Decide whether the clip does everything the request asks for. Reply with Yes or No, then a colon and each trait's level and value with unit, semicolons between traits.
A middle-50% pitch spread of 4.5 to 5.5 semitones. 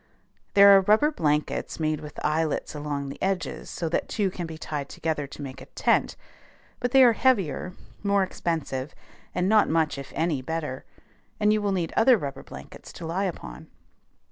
Yes: average, 5.2 semitones